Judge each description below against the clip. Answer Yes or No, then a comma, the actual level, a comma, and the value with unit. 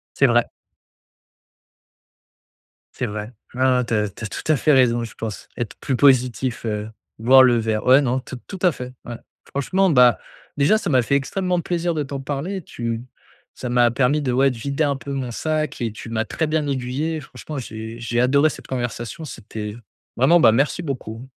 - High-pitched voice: No, low, 130 Hz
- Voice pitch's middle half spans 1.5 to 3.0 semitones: No, average, 3.5 semitones